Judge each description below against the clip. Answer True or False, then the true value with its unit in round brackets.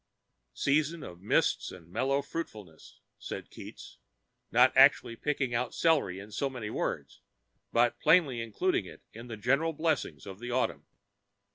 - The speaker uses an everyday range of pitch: False (5.8 semitones)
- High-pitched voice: False (120 Hz)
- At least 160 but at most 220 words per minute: False (145 wpm)